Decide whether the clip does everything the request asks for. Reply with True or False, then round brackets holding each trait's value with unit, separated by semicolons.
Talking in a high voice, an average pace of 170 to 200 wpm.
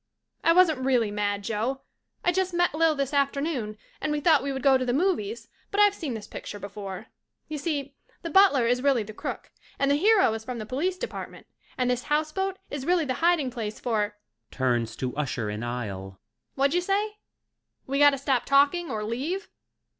True (270 Hz; 195 wpm)